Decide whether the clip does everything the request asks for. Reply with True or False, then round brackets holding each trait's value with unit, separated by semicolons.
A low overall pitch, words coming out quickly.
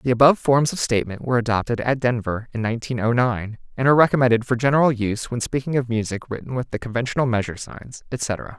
True (120 Hz; 210 wpm)